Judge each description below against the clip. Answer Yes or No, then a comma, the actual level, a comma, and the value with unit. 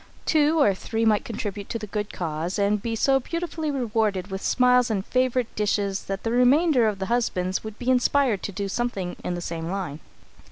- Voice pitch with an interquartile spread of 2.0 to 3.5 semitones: No, average, 4.4 semitones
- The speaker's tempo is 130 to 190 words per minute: No, average, 200 wpm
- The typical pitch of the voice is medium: No, high, 215 Hz